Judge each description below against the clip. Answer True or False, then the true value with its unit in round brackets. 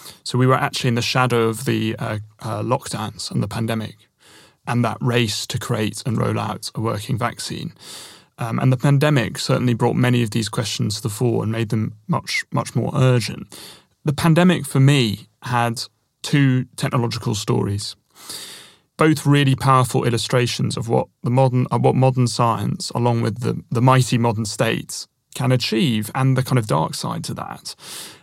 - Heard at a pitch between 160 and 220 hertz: False (120 Hz)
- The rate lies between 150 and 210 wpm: True (175 wpm)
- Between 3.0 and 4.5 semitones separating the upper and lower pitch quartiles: False (2.5 semitones)